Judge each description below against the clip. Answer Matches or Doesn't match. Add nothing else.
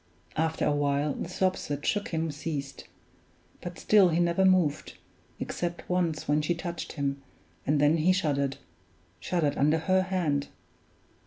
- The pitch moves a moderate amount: Matches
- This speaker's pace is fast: Doesn't match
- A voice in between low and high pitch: Matches